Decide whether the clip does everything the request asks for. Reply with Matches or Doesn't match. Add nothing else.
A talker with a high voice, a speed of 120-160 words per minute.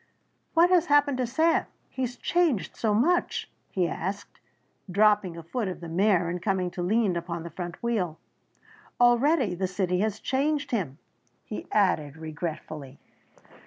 Matches